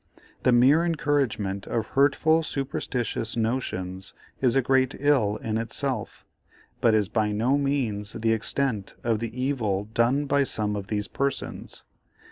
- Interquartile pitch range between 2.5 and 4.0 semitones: No, average, 4.4 semitones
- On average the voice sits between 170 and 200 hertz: No, low, 120 Hz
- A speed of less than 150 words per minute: Yes, average, 140 wpm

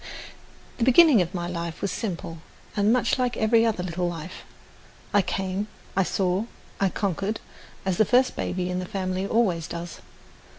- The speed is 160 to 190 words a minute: Yes, average, 165 wpm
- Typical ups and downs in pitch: Yes, average, 3.5 semitones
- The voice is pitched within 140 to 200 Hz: Yes, high, 190 Hz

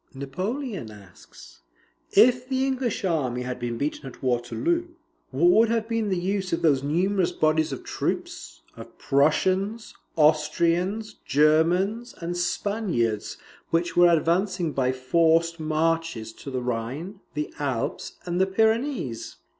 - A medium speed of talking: No, slow, 130 wpm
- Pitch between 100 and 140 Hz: No, medium, 170 Hz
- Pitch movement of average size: No, wide, 6.4 semitones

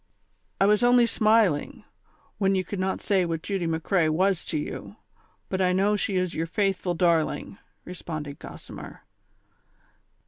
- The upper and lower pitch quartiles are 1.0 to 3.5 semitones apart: Yes, average, 3.2 semitones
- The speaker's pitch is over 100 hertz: Yes, medium, 185 Hz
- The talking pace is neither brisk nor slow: Yes, average, 150 wpm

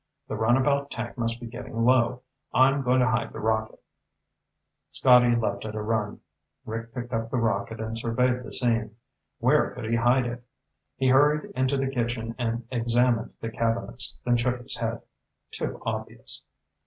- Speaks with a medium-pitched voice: No, low, 120 Hz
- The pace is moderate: Yes, average, 165 wpm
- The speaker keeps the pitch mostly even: Yes, narrow, 1.8 semitones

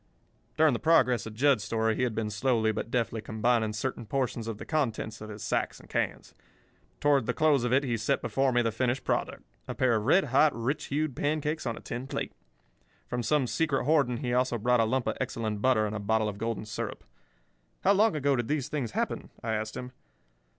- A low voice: Yes, low, 120 Hz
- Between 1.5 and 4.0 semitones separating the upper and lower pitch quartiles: Yes, average, 3.7 semitones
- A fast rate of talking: Yes, fast, 220 wpm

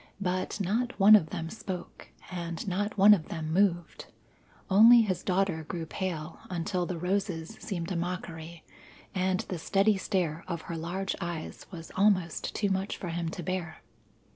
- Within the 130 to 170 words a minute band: Yes, average, 165 wpm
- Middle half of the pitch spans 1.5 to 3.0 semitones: Yes, narrow, 2.6 semitones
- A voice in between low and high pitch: Yes, medium, 180 Hz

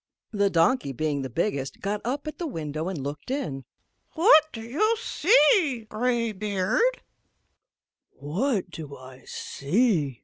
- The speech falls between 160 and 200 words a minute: No, average, 145 wpm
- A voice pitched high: Yes, high, 200 Hz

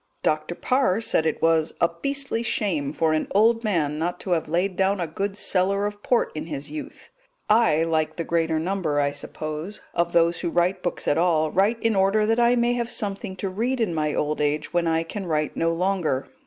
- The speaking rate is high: Yes, fast, 215 wpm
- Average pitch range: Yes, average, 4.6 semitones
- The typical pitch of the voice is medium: Yes, medium, 175 Hz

